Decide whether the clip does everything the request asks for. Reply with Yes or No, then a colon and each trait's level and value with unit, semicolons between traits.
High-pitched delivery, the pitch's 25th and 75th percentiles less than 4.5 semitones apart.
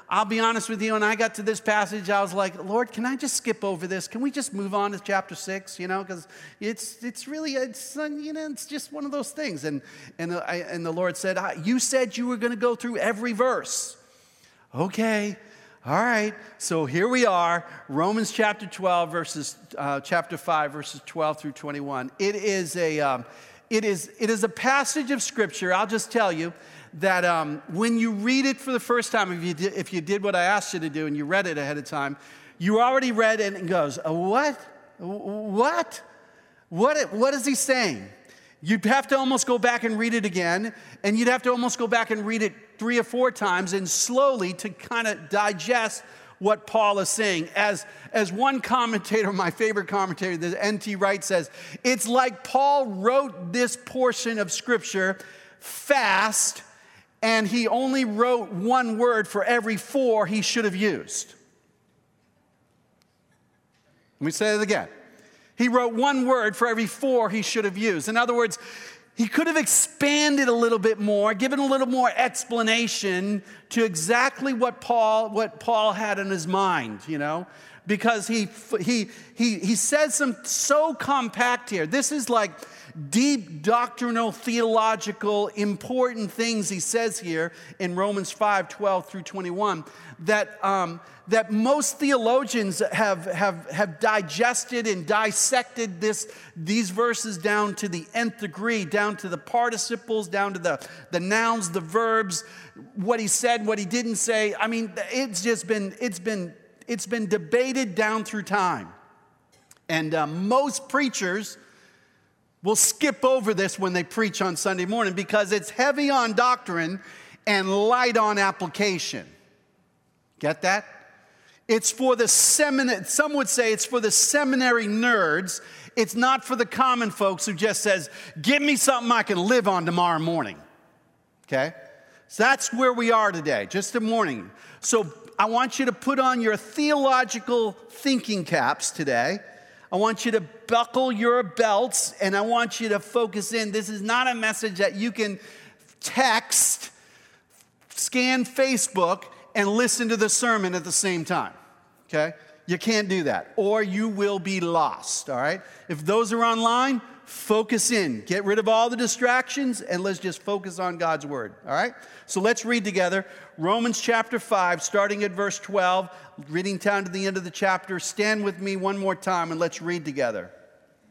Yes: high, 215 Hz; average, 3.9 semitones